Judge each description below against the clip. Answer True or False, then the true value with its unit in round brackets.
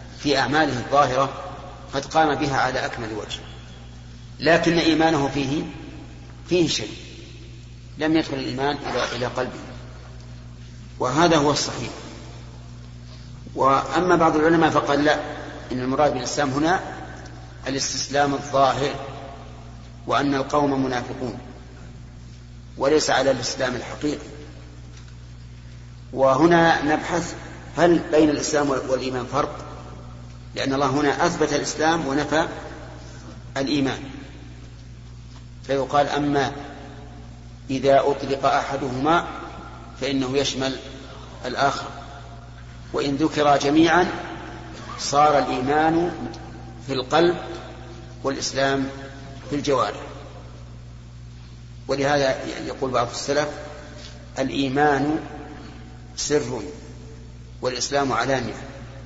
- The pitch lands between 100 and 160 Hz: True (135 Hz)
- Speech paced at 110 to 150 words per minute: False (80 wpm)